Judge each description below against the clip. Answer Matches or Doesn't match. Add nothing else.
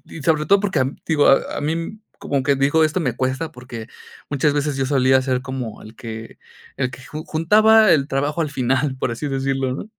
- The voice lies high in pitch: Doesn't match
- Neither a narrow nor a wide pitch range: Matches